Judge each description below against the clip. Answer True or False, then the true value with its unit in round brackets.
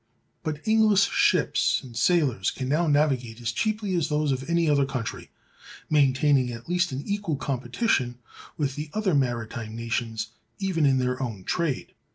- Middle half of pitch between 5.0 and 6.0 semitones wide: True (5.5 semitones)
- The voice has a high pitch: False (140 Hz)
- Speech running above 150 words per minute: True (160 wpm)